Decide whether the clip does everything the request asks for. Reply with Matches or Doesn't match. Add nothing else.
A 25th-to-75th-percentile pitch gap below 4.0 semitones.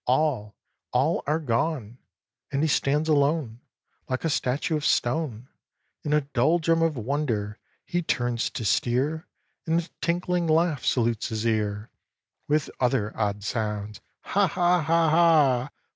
Doesn't match